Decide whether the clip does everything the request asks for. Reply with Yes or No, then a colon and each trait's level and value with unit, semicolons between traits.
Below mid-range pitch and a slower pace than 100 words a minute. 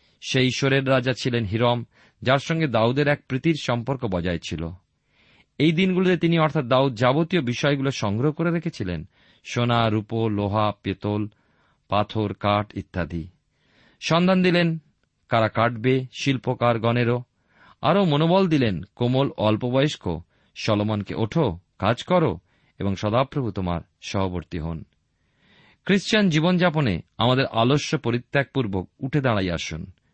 No: low, 120 Hz; average, 115 wpm